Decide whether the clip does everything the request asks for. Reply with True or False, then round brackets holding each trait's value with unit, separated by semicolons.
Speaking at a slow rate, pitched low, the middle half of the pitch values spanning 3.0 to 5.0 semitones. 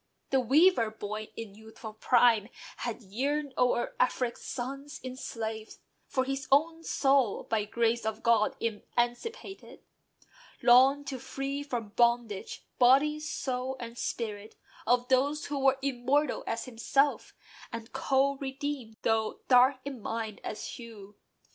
False (130 wpm; 245 Hz; 3.4 semitones)